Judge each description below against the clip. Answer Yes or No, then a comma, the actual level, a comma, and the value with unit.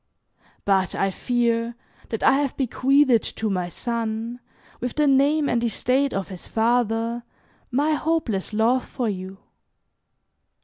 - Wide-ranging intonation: No, average, 3.4 semitones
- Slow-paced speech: Yes, slow, 130 wpm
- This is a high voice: Yes, high, 235 Hz